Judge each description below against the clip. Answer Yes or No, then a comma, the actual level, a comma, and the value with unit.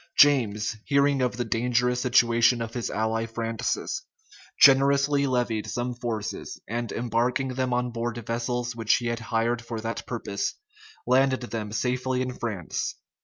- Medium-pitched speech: No, low, 120 Hz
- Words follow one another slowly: No, average, 145 wpm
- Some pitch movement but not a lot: No, narrow, 1.8 semitones